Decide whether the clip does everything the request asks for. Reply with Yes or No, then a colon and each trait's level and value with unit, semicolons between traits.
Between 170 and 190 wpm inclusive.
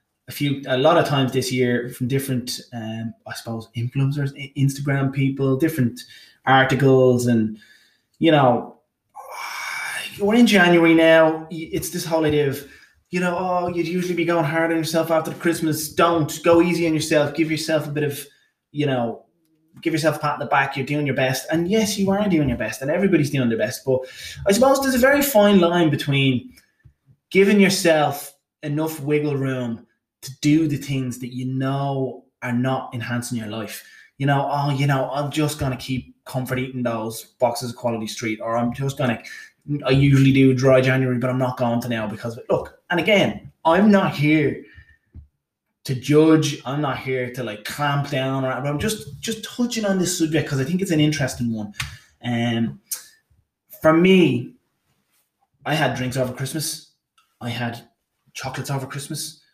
Yes: average, 185 wpm